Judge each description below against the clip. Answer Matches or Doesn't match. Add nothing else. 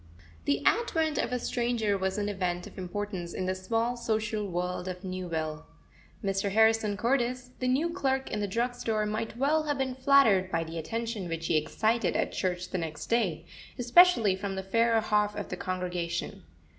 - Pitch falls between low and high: Doesn't match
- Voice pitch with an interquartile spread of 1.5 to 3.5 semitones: Doesn't match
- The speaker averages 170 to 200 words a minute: Matches